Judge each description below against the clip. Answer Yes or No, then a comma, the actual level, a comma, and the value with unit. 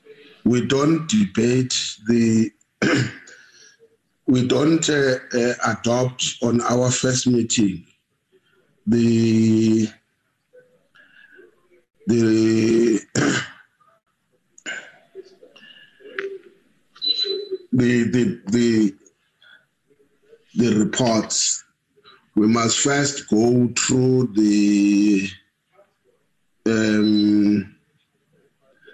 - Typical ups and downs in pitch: No, wide, 6.0 semitones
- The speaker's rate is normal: No, slow, 60 wpm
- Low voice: Yes, low, 120 Hz